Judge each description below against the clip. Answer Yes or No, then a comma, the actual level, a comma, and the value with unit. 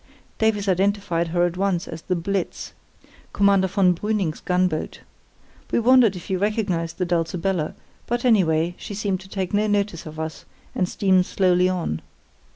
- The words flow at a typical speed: Yes, average, 160 wpm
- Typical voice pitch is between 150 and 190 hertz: Yes, medium, 185 Hz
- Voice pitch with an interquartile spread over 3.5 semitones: No, average, 2.8 semitones